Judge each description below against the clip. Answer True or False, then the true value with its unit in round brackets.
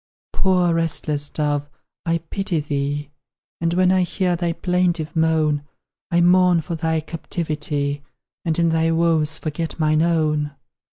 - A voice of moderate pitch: True (160 Hz)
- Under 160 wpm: True (135 wpm)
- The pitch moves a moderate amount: False (2.1 semitones)